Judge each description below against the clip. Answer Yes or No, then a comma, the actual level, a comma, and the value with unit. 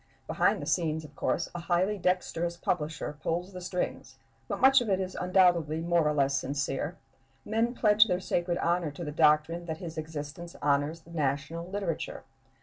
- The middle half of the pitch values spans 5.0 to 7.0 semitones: No, average, 3.0 semitones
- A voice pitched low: No, medium, 170 Hz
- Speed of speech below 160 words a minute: No, average, 175 wpm